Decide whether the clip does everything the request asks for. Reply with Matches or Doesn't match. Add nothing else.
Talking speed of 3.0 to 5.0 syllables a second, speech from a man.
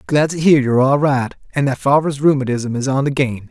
Doesn't match